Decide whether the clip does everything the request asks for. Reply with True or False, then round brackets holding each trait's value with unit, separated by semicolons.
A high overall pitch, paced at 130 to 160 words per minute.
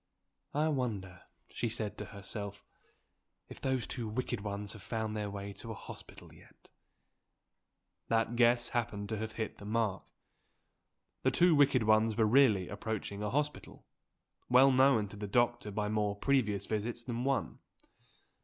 False (110 Hz; 155 wpm)